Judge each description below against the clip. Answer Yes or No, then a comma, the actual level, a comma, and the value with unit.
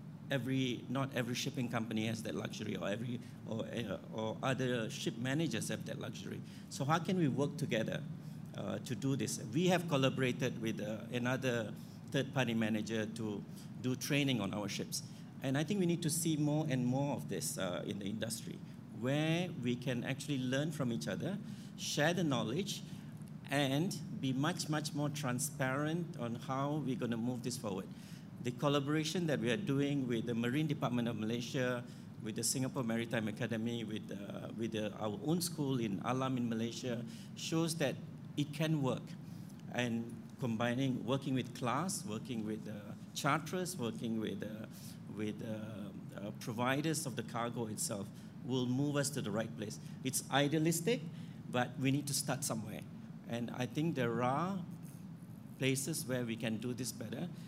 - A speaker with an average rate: Yes, average, 170 wpm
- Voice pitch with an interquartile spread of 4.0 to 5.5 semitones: Yes, average, 5.2 semitones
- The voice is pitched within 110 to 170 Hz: Yes, low, 135 Hz